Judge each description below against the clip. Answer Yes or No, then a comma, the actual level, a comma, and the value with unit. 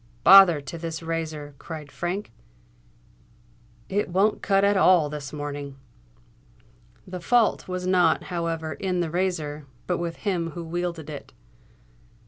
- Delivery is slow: Yes, slow, 130 wpm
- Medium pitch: Yes, medium, 170 Hz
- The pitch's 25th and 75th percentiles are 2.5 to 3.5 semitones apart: Yes, average, 3.0 semitones